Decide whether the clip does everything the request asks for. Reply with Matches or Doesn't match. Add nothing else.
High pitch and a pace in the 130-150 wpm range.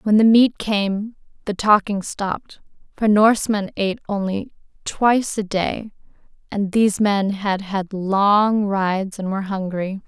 Matches